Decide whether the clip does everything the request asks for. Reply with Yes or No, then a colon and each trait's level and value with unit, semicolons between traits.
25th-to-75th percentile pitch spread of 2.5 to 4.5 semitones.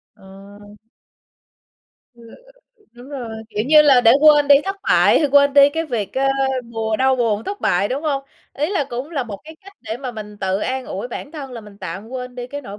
No: average, 5.1 semitones